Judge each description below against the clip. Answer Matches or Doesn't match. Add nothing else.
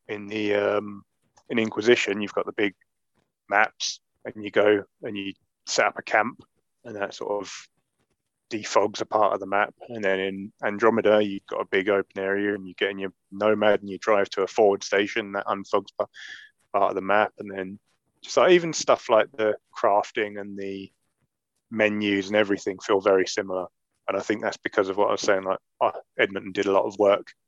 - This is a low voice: Matches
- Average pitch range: Doesn't match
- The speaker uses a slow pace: Doesn't match